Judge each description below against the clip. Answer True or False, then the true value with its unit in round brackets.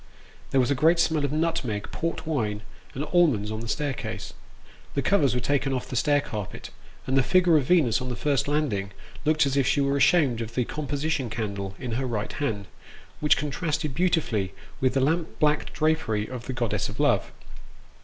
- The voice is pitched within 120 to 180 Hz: True (135 Hz)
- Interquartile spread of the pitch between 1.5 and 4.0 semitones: False (4.6 semitones)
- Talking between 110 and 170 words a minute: False (195 wpm)